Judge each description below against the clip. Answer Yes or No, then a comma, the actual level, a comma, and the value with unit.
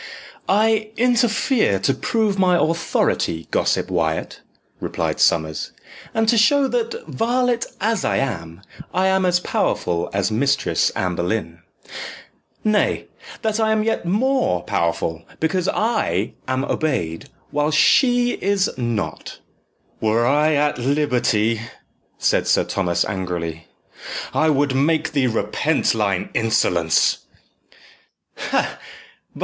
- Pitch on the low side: No, medium, 150 Hz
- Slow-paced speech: Yes, slow, 115 wpm